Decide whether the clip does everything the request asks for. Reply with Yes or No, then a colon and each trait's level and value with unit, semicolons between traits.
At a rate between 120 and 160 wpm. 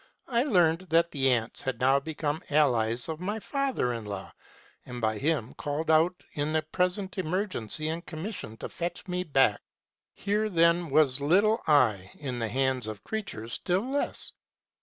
No: average, 170 wpm